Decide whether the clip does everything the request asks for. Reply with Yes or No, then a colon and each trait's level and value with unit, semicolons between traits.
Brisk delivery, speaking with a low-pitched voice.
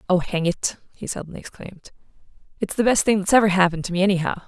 No: fast, 215 wpm; high, 190 Hz